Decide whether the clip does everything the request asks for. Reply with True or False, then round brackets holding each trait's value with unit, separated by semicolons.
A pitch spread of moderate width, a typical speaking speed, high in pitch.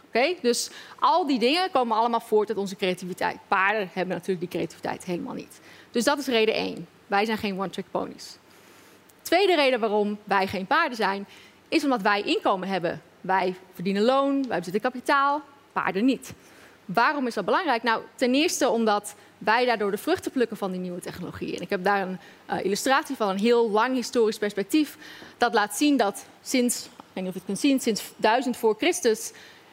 True (4.6 semitones; 185 wpm; 220 Hz)